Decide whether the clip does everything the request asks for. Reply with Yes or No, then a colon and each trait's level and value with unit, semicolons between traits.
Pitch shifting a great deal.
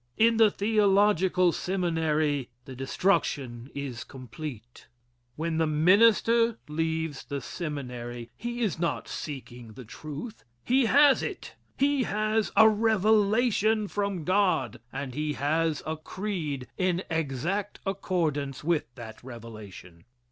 Yes: wide, 7.1 semitones